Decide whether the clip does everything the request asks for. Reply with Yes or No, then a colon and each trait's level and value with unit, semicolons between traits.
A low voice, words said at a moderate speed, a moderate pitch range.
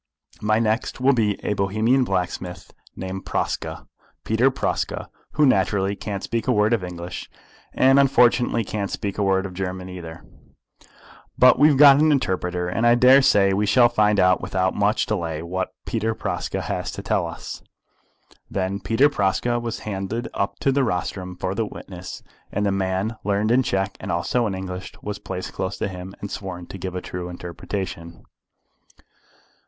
Yes: low, 100 Hz; average, 170 wpm; average, 3.9 semitones